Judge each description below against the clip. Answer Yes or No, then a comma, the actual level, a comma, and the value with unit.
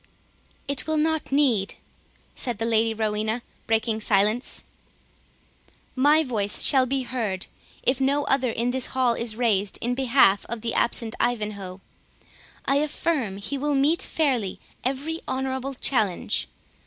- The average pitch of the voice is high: Yes, high, 245 Hz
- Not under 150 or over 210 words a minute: No, slow, 135 wpm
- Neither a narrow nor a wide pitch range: Yes, average, 3.9 semitones